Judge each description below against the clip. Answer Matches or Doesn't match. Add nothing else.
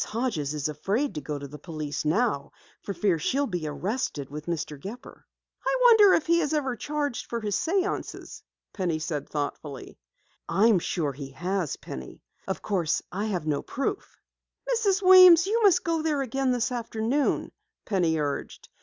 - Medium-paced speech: Matches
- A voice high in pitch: Matches